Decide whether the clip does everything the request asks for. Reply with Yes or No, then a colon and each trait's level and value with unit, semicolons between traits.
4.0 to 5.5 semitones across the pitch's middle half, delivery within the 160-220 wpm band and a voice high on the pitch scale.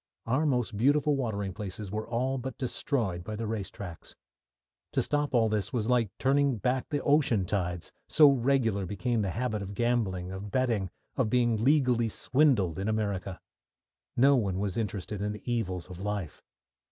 No: average, 4.4 semitones; average, 170 wpm; low, 110 Hz